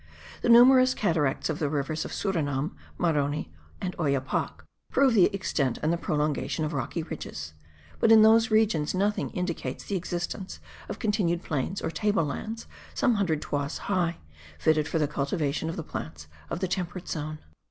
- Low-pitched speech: No, medium, 165 Hz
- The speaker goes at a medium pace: Yes, average, 165 wpm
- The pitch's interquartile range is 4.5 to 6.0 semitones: Yes, average, 5.2 semitones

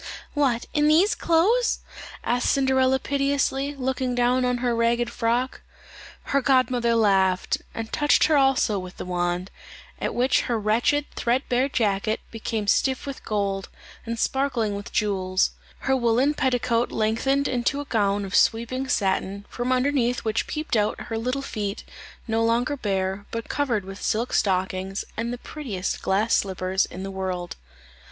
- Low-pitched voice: No, high, 235 Hz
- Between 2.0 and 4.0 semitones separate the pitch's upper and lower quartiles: No, average, 4.7 semitones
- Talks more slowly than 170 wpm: Yes, average, 155 wpm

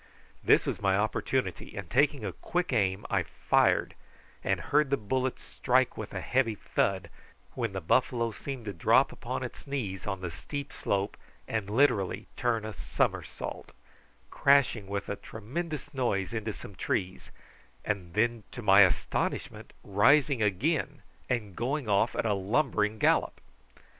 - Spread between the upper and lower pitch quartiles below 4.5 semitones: No, average, 4.9 semitones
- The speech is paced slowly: No, average, 150 wpm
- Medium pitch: No, low, 110 Hz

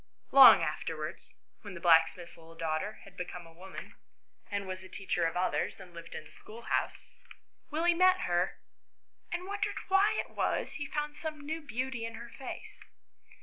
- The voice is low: No, high, 200 Hz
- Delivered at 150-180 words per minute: Yes, average, 170 wpm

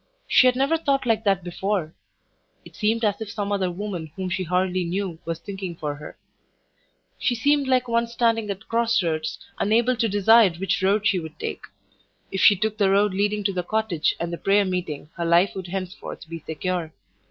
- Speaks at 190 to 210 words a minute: Yes, average, 200 wpm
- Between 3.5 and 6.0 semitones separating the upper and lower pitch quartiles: Yes, average, 3.9 semitones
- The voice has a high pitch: Yes, high, 195 Hz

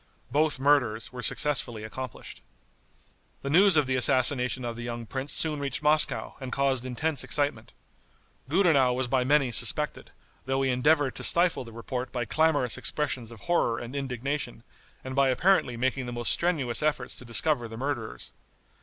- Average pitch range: Yes, average, 3.3 semitones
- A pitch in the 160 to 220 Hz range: No, low, 130 Hz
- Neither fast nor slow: Yes, average, 165 wpm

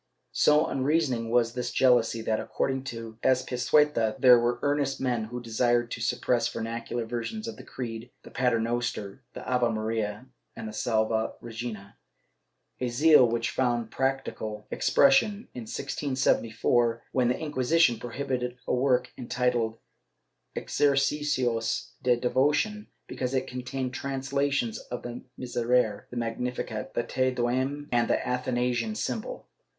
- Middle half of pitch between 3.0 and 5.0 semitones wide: No, narrow, 2.4 semitones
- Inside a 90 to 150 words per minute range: Yes, slow, 135 wpm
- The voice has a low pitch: Yes, low, 125 Hz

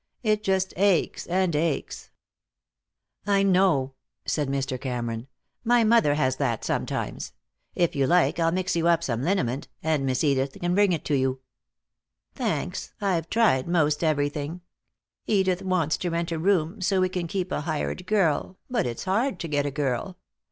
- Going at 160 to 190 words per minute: Yes, average, 165 wpm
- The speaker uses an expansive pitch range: No, average, 4.8 semitones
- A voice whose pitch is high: No, medium, 170 Hz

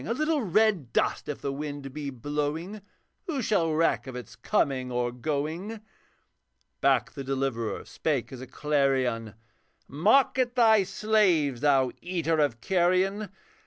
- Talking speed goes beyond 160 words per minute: No, average, 140 wpm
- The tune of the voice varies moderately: No, wide, 6.6 semitones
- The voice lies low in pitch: No, medium, 150 Hz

